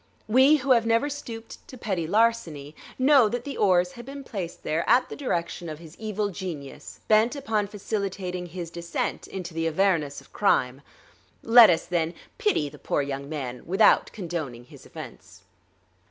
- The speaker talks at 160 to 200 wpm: Yes, average, 170 wpm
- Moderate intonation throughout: No, wide, 5.8 semitones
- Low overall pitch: No, high, 190 Hz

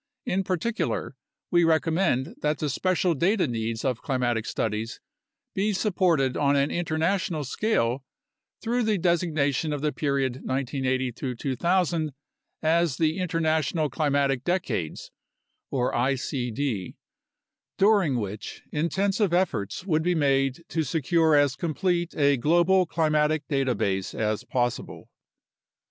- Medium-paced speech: No, slow, 120 wpm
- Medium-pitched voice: Yes, medium, 150 Hz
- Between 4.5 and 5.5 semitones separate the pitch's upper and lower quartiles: Yes, average, 4.8 semitones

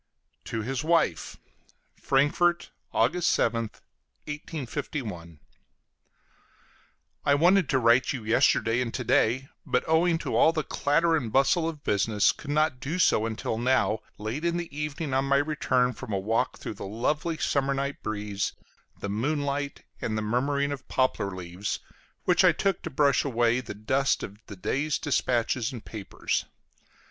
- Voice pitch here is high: No, low, 130 Hz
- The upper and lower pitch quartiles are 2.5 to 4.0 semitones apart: No, average, 5.0 semitones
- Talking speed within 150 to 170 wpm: Yes, average, 155 wpm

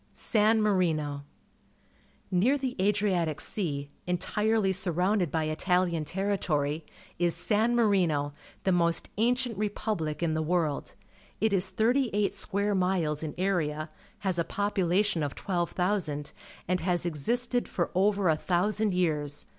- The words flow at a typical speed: No, slow, 130 wpm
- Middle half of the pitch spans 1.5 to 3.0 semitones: No, average, 4.5 semitones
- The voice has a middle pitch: Yes, medium, 180 Hz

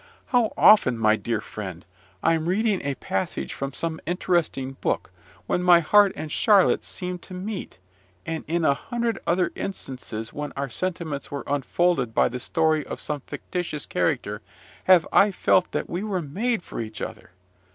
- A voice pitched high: No, medium, 165 Hz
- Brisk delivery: No, average, 165 wpm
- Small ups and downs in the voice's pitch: No, average, 5.2 semitones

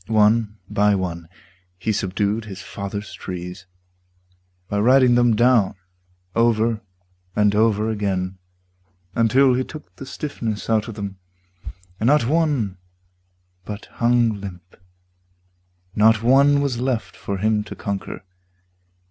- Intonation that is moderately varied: Yes, average, 3.0 semitones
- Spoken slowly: Yes, slow, 120 wpm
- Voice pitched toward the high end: No, low, 110 Hz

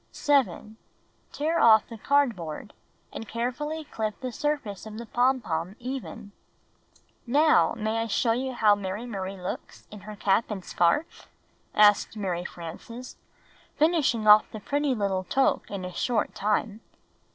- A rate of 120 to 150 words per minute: Yes, average, 140 wpm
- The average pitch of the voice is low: No, high, 220 Hz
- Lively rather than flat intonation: No, average, 4.2 semitones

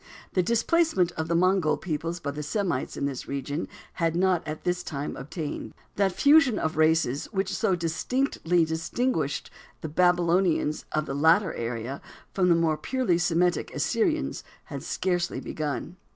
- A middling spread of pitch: Yes, average, 3.5 semitones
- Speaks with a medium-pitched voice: Yes, medium, 170 Hz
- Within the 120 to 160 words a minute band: Yes, average, 150 wpm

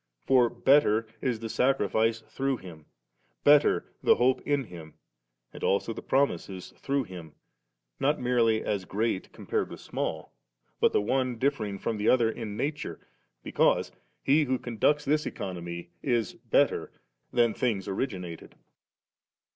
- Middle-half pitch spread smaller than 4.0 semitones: No, average, 5.3 semitones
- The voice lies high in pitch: No, low, 115 Hz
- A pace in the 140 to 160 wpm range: Yes, average, 145 wpm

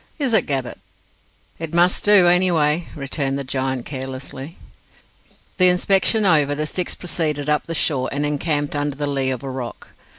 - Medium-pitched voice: Yes, medium, 150 Hz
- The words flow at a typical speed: Yes, average, 170 wpm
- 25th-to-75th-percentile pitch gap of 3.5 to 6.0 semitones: Yes, average, 4.2 semitones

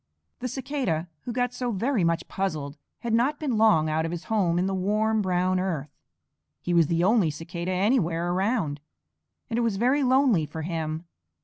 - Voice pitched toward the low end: No, medium, 185 Hz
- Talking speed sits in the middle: Yes, average, 185 wpm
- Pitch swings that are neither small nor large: No, wide, 5.9 semitones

